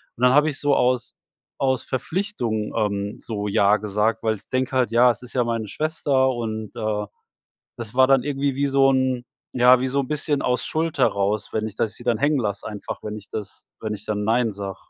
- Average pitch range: Yes, average, 3.7 semitones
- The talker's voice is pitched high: No, low, 120 Hz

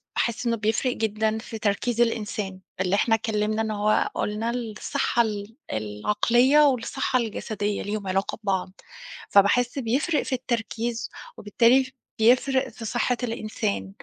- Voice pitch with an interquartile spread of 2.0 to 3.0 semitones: Yes, narrow, 2.6 semitones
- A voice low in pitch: No, high, 225 Hz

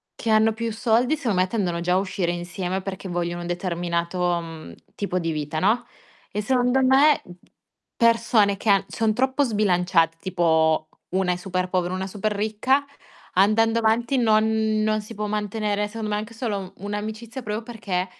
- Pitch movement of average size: Yes, average, 3.7 semitones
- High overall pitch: Yes, high, 205 Hz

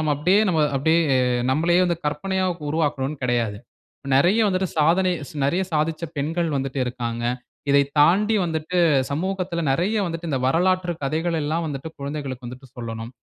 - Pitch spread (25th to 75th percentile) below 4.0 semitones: No, average, 4.4 semitones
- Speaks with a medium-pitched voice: Yes, medium, 155 Hz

